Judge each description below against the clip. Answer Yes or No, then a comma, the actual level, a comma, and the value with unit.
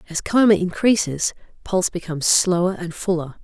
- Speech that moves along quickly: No, average, 140 wpm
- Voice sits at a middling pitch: Yes, medium, 180 Hz